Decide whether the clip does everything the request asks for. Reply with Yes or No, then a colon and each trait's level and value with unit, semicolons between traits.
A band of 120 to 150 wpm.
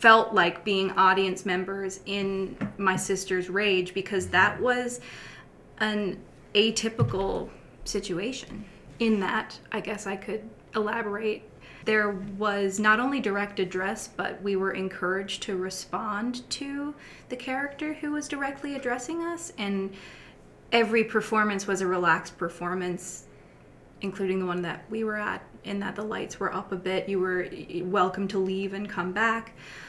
Yes: average, 145 wpm